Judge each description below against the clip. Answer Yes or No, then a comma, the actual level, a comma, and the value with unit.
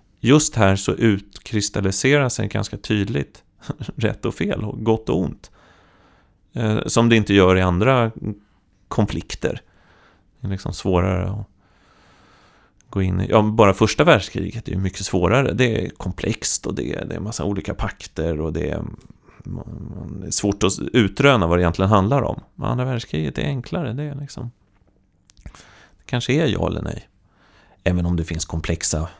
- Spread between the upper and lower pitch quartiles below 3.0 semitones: No, average, 3.8 semitones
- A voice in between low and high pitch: No, low, 100 Hz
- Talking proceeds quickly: No, average, 160 wpm